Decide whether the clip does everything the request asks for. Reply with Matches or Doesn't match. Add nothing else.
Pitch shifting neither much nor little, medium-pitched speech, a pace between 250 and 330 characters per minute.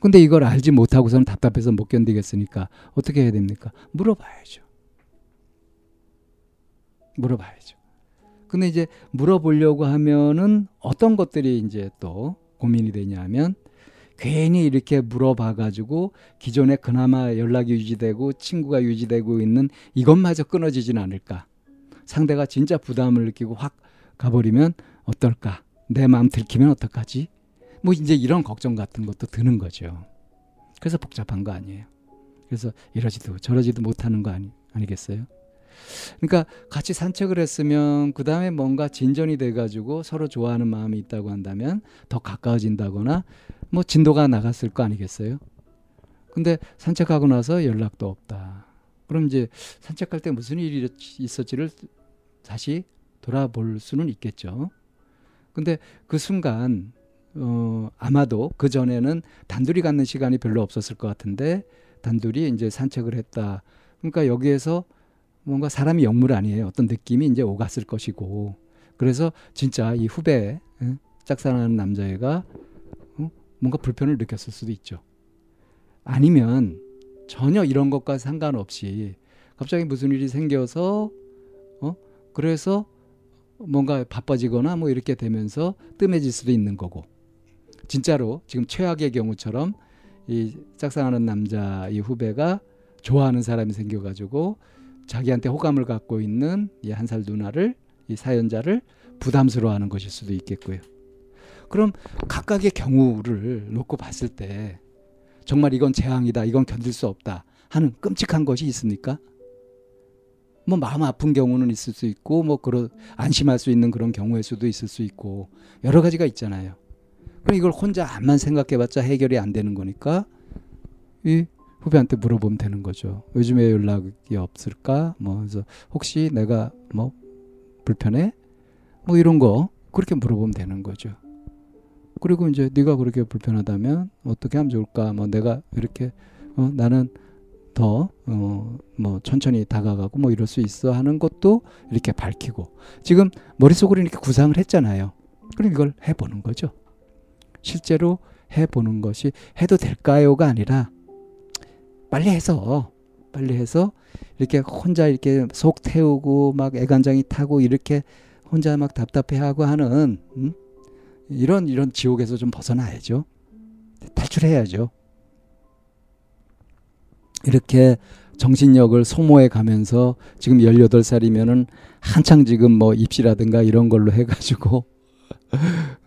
Doesn't match